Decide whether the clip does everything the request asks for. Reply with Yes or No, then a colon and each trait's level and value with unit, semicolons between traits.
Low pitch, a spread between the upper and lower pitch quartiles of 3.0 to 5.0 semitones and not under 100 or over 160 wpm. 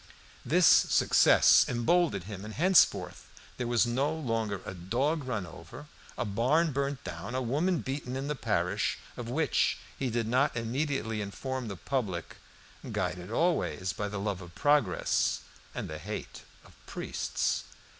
No: low, 120 Hz; wide, 5.5 semitones; average, 150 wpm